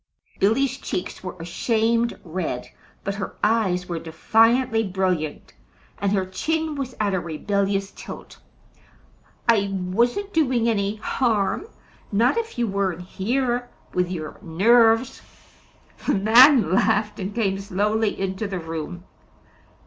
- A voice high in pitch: Yes, high, 205 Hz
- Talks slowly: Yes, slow, 125 wpm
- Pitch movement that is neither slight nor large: Yes, average, 4.0 semitones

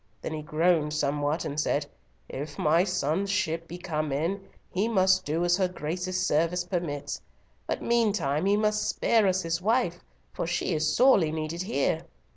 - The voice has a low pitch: No, medium, 175 Hz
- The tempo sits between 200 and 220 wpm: No, average, 170 wpm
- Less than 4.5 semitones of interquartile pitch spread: Yes, average, 3.6 semitones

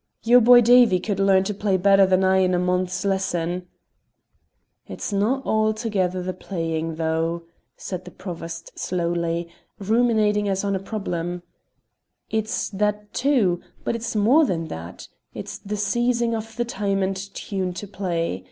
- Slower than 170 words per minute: Yes, average, 150 wpm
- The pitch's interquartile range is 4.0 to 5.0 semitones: No, average, 3.4 semitones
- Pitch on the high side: Yes, high, 195 Hz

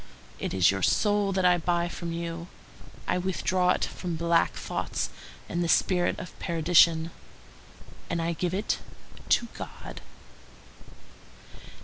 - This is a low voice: No, medium, 170 Hz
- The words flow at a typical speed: No, slow, 130 wpm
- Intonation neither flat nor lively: No, narrow, 1.5 semitones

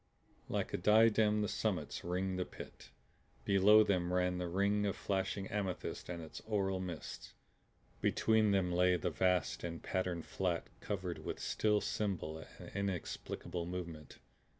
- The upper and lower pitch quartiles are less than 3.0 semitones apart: Yes, narrow, 2.5 semitones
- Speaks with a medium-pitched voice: No, very low, 95 Hz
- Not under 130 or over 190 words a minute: Yes, average, 145 wpm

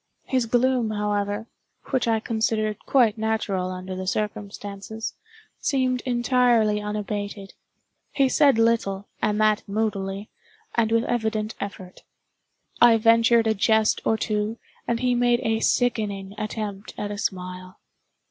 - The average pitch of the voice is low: No, high, 215 Hz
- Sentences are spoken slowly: Yes, slow, 130 wpm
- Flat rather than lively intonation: Yes, narrow, 2.3 semitones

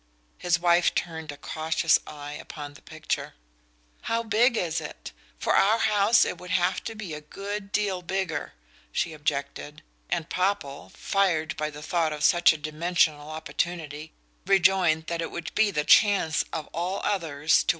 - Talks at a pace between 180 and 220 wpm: No, average, 165 wpm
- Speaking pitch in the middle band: Yes, medium, 170 Hz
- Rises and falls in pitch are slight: No, average, 4.0 semitones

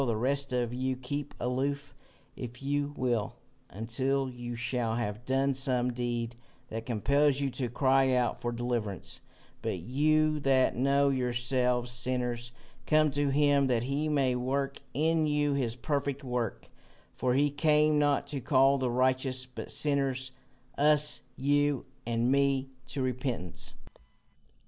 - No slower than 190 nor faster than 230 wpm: No, average, 140 wpm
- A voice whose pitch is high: No, low, 130 Hz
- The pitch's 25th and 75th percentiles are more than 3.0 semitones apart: No, narrow, 2.4 semitones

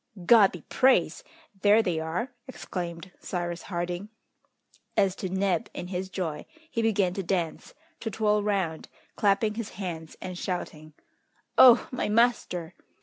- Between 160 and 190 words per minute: No, average, 140 wpm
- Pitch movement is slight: No, average, 3.4 semitones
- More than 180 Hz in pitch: Yes, high, 190 Hz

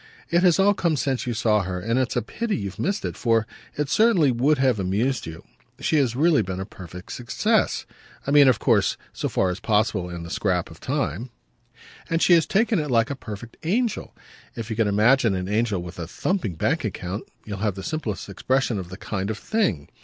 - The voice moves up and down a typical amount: No, wide, 7.3 semitones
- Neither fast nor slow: No, fast, 215 wpm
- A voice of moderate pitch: No, low, 115 Hz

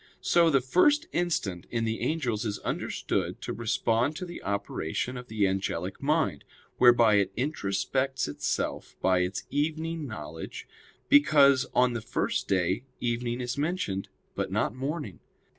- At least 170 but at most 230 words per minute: No, average, 140 wpm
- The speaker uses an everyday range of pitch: No, wide, 6.4 semitones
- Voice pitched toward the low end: Yes, low, 120 Hz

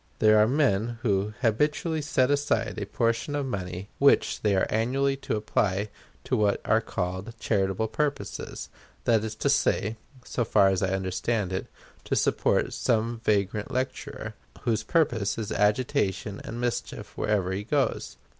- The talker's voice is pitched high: No, low, 110 Hz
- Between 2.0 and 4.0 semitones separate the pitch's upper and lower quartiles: Yes, average, 3.7 semitones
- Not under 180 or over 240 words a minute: No, average, 155 wpm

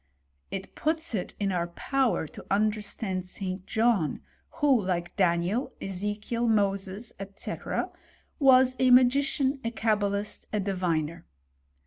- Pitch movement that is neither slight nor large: Yes, average, 4.6 semitones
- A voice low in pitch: No, high, 205 Hz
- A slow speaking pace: Yes, slow, 120 wpm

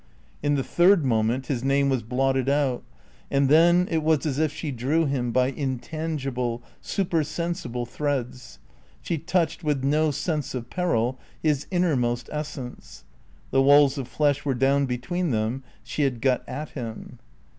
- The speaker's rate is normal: Yes, average, 155 wpm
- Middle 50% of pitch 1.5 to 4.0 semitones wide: Yes, average, 3.5 semitones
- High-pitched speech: No, medium, 140 Hz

